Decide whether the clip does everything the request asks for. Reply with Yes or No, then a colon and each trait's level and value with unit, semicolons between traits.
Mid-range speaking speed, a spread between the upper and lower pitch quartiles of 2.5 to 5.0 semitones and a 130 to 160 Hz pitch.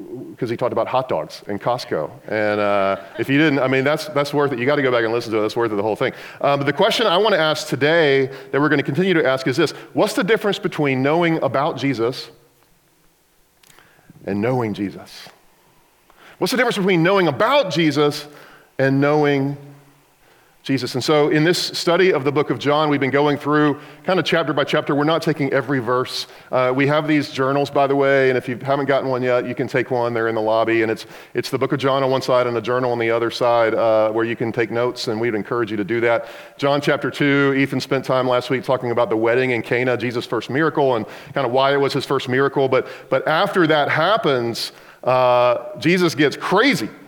No: fast, 235 wpm; average, 3.3 semitones; low, 135 Hz